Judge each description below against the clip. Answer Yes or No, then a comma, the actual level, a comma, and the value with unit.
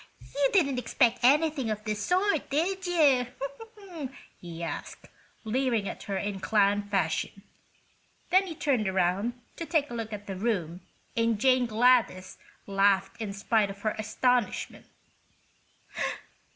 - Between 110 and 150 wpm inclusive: Yes, slow, 135 wpm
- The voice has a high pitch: Yes, high, 230 Hz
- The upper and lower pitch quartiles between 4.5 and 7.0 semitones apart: Yes, wide, 5.5 semitones